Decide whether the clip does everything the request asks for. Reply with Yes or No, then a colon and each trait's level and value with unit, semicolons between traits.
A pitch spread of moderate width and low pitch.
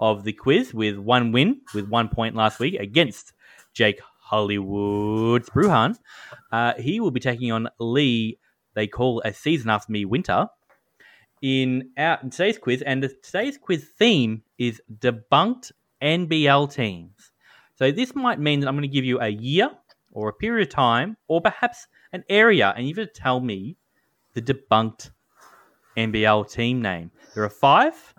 Yes: average, 5.0 semitones; low, 125 Hz